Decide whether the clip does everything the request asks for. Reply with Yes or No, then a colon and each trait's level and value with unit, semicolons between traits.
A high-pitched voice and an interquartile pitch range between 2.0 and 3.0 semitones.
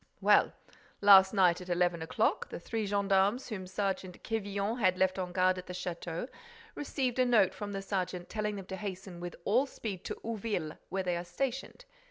Yes: high, 195 Hz; average, 2.7 semitones